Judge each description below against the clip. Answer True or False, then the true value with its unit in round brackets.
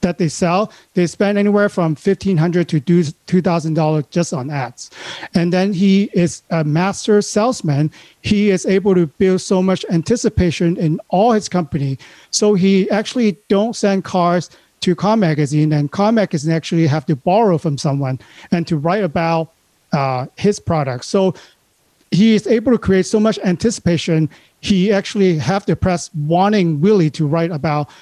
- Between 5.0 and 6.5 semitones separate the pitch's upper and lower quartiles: False (3.7 semitones)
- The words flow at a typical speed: True (165 wpm)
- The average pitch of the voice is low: False (180 Hz)